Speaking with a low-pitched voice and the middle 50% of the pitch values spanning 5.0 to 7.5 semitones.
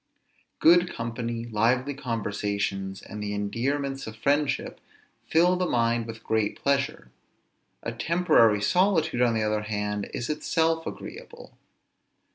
Yes: low, 115 Hz; wide, 5.5 semitones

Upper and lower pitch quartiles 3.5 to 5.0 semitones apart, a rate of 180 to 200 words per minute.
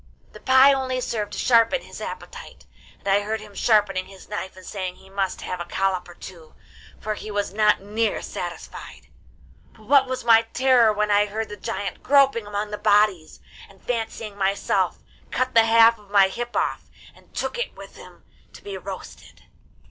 No: average, 3.0 semitones; average, 185 wpm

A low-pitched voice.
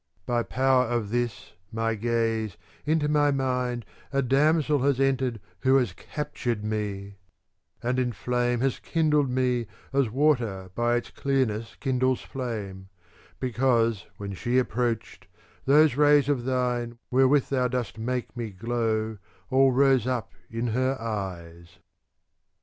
Yes: low, 125 Hz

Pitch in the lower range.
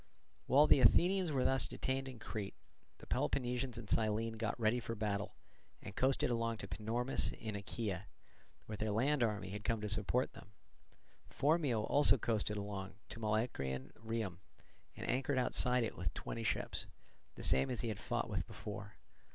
Yes: low, 115 Hz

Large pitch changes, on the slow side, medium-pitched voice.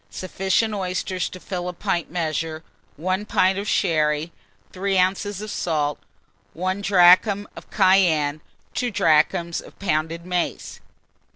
No: average, 3.0 semitones; slow, 125 wpm; medium, 180 Hz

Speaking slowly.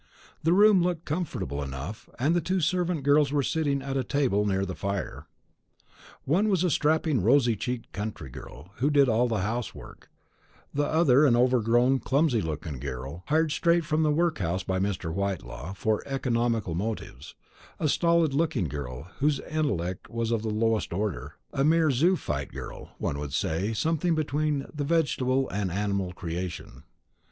No: average, 165 wpm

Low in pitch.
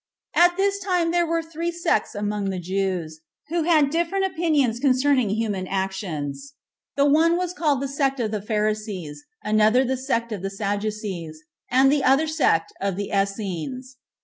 No: high, 245 Hz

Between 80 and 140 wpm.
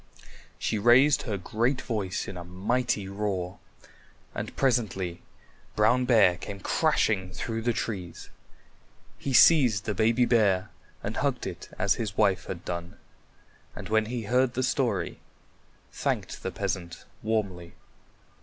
Yes: slow, 135 wpm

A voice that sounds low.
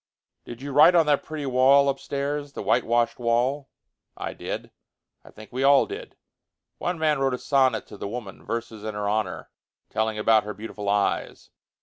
Yes: low, 125 Hz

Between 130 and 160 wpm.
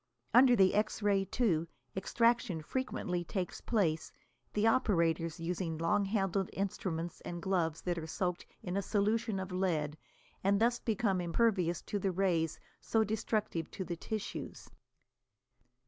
Yes: average, 140 wpm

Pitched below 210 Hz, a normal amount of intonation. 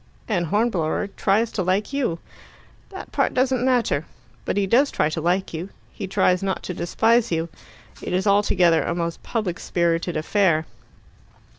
Yes: high, 190 Hz; average, 4.5 semitones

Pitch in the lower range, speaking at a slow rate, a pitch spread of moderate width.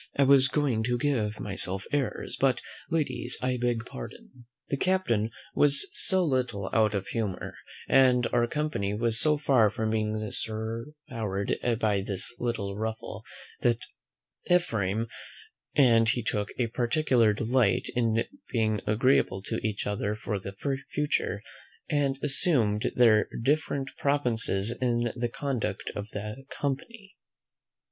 Yes: low, 115 Hz; slow, 130 wpm; average, 4.1 semitones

